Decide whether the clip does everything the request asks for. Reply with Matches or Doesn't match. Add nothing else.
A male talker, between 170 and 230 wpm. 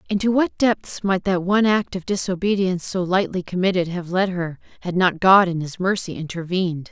Doesn't match